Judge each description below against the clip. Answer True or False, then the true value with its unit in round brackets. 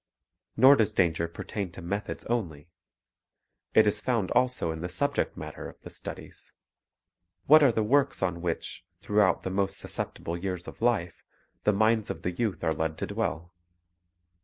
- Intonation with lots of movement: False (4.5 semitones)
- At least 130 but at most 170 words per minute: True (165 wpm)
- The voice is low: True (95 Hz)